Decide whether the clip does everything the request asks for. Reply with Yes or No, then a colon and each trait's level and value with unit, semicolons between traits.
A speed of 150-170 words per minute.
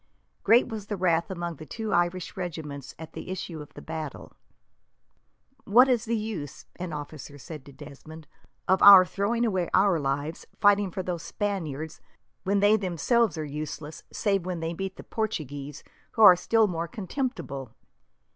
Yes: average, 165 wpm